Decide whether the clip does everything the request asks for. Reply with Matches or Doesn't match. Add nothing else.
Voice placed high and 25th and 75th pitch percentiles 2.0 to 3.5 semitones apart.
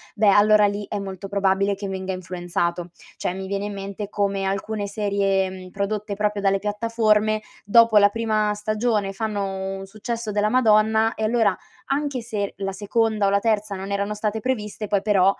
Doesn't match